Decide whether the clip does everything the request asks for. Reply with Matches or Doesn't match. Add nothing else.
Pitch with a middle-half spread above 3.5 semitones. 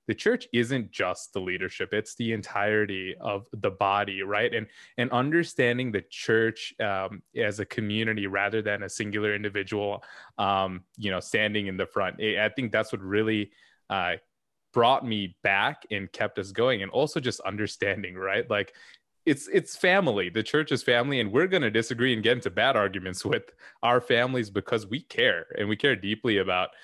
Doesn't match